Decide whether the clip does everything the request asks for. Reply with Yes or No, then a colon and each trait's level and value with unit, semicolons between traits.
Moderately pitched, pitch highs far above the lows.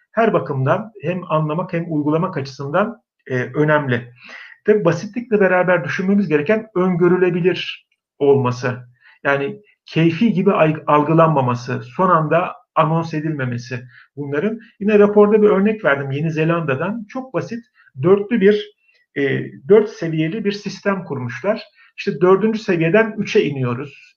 Yes: medium, 175 Hz; wide, 6.0 semitones